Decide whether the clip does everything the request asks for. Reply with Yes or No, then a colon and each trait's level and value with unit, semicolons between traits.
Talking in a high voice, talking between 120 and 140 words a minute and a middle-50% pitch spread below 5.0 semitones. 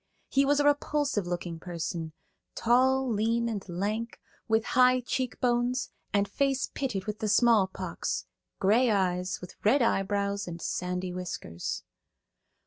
No: high, 215 Hz; slow, 135 wpm; average, 5.3 semitones